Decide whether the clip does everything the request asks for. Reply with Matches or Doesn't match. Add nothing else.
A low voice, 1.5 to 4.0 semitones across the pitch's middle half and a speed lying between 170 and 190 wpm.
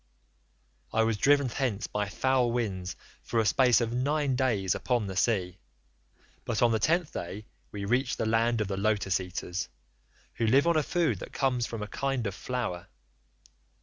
Doesn't match